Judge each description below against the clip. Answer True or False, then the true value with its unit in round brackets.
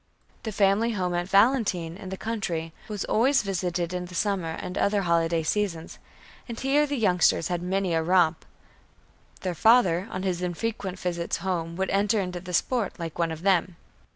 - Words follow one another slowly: False (180 wpm)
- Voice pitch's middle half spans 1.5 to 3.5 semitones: True (3.2 semitones)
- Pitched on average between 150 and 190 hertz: True (185 Hz)